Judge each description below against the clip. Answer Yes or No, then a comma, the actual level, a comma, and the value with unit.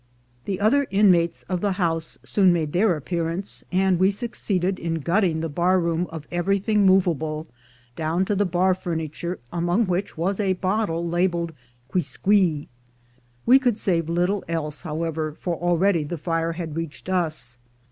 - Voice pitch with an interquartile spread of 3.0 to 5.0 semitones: No, narrow, 2.6 semitones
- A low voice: No, medium, 175 Hz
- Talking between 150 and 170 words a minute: Yes, average, 155 wpm